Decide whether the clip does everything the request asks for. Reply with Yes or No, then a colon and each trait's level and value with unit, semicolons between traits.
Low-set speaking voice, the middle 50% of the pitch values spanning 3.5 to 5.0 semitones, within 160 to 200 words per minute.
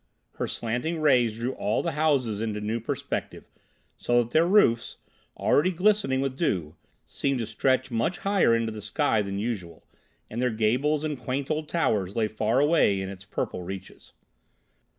No: low, 120 Hz; wide, 5.6 semitones; average, 170 wpm